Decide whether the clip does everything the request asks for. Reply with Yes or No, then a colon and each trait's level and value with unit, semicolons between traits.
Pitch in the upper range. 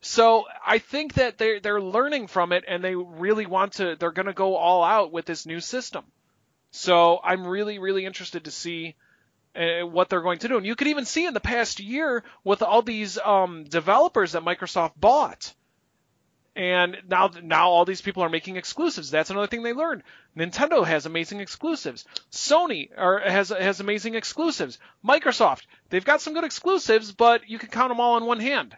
Yes: high, 200 Hz